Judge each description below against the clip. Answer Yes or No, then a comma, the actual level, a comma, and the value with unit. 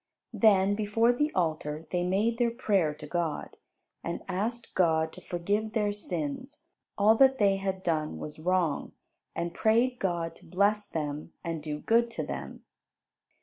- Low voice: No, high, 190 Hz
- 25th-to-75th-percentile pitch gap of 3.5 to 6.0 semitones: Yes, average, 4.9 semitones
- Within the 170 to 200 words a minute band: No, average, 155 wpm